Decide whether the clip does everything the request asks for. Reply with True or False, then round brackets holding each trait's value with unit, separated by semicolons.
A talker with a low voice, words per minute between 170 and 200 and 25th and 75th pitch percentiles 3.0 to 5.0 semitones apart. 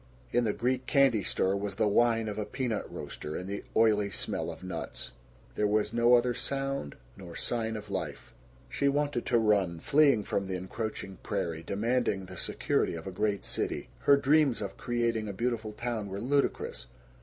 True (110 Hz; 180 wpm; 3.7 semitones)